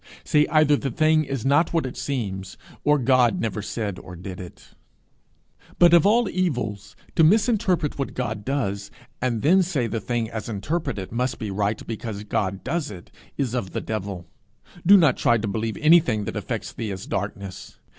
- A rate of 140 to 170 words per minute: No, average, 180 wpm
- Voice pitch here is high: No, low, 120 Hz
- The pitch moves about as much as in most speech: No, wide, 7.0 semitones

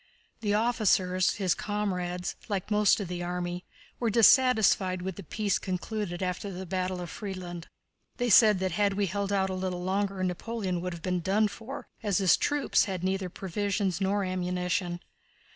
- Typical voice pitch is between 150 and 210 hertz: Yes, high, 190 Hz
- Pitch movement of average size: No, narrow, 2.3 semitones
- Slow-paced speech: No, average, 170 wpm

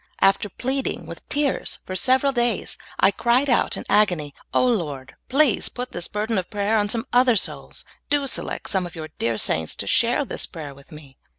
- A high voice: Yes, high, 210 Hz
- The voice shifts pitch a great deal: Yes, wide, 7.1 semitones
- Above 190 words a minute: Yes, average, 200 wpm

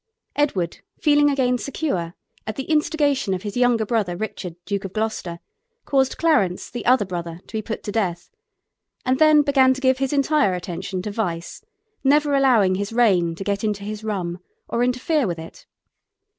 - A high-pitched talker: Yes, high, 220 Hz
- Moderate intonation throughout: No, wide, 6.4 semitones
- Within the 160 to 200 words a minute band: Yes, average, 175 wpm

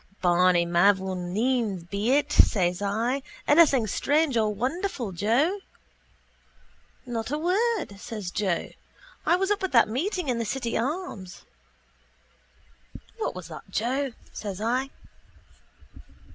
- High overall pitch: Yes, high, 230 Hz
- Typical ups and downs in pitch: No, wide, 6.8 semitones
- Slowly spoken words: Yes, slow, 115 wpm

